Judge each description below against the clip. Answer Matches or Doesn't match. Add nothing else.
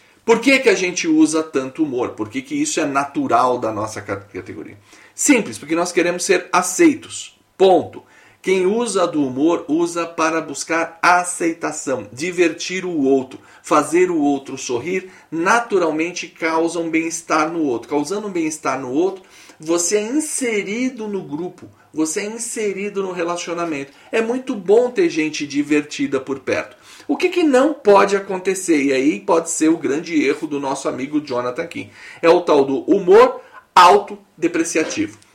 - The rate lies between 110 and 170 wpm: Matches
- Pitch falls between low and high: Matches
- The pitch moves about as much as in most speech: Doesn't match